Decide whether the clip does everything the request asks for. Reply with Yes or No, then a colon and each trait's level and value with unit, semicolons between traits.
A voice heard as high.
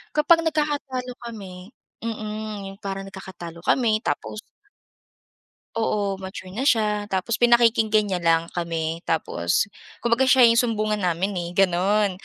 Yes: high, 210 Hz